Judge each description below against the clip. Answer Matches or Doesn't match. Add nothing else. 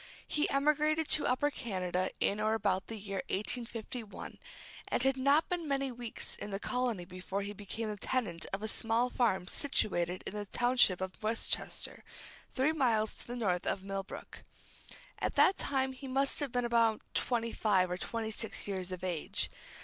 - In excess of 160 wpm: Matches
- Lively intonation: Doesn't match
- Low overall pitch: Doesn't match